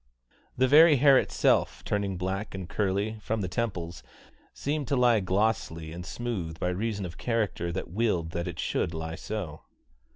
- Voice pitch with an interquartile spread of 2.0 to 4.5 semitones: No, average, 4.9 semitones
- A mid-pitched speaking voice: No, very low, 95 Hz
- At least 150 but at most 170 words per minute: Yes, average, 165 wpm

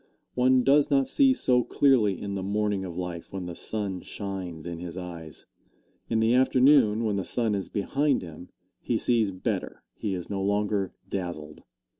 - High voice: No, low, 100 Hz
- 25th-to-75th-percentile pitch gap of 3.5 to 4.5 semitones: No, average, 5.2 semitones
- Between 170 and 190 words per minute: Yes, average, 175 wpm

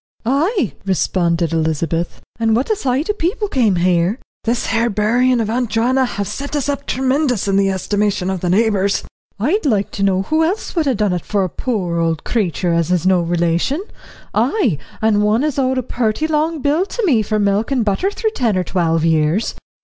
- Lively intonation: Yes, wide, 6.4 semitones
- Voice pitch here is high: Yes, high, 215 Hz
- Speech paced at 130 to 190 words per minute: No, fast, 205 wpm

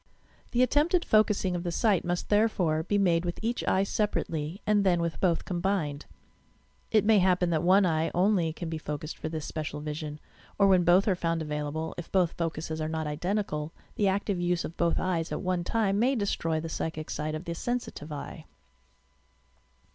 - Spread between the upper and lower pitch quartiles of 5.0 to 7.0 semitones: No, average, 3.9 semitones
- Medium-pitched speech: Yes, medium, 175 Hz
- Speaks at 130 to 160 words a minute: No, average, 195 wpm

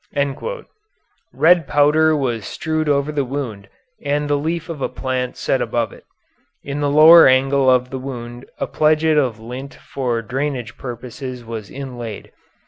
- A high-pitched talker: No, low, 135 Hz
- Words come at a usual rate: Yes, average, 150 wpm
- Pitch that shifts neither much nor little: Yes, average, 3.2 semitones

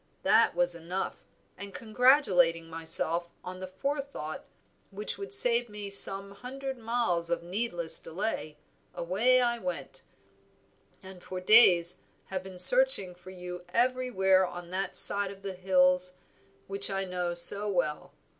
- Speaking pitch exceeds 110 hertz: Yes, high, 190 Hz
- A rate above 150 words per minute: No, average, 140 wpm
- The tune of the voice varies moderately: Yes, average, 4.4 semitones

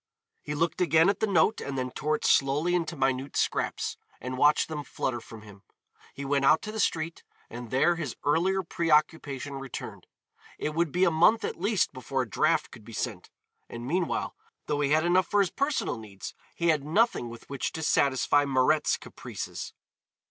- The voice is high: No, medium, 150 Hz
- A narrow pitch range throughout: No, average, 4.2 semitones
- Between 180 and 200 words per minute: Yes, average, 190 wpm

